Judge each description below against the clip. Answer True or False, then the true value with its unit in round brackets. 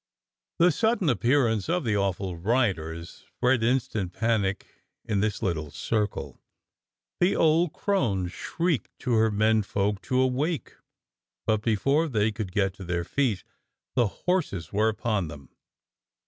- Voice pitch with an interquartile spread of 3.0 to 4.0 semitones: False (5.3 semitones)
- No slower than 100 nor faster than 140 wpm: True (135 wpm)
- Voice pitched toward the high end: False (110 Hz)